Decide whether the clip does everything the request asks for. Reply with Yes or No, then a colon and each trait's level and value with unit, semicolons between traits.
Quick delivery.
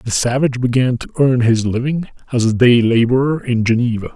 No: average, 190 wpm